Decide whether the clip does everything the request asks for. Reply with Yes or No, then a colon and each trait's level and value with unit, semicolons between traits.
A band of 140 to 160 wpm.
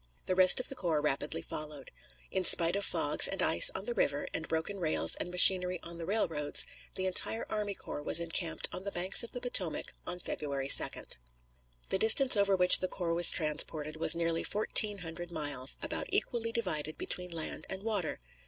No: average, 190 wpm